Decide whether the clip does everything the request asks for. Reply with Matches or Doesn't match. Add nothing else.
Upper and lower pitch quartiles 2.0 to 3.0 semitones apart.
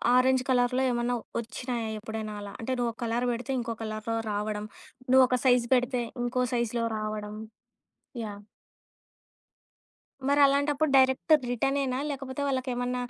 Matches